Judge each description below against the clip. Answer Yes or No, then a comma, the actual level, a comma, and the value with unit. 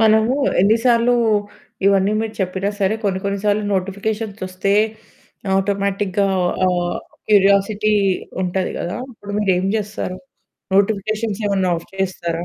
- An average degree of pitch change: No, narrow, 2.1 semitones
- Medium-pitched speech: No, high, 200 Hz